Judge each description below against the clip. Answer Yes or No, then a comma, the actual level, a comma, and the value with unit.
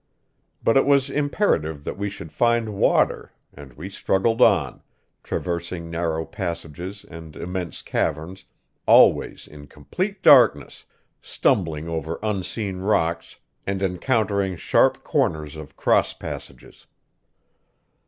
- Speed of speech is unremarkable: No, slow, 115 wpm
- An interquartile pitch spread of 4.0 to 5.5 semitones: Yes, average, 4.7 semitones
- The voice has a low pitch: Yes, very low, 90 Hz